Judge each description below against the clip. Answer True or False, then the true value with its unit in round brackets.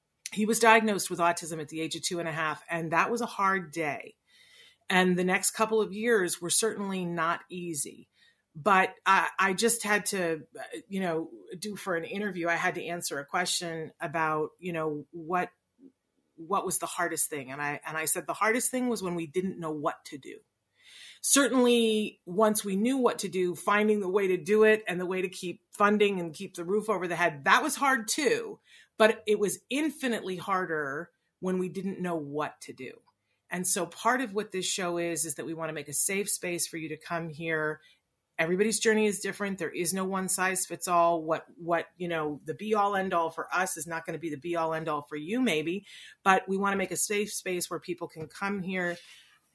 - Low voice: False (185 Hz)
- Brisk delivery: True (225 wpm)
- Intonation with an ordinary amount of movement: True (3.8 semitones)